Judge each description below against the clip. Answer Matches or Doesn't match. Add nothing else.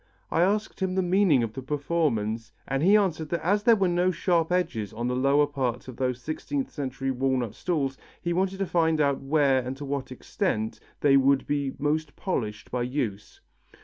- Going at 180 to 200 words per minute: Matches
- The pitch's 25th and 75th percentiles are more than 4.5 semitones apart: Matches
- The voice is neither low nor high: Matches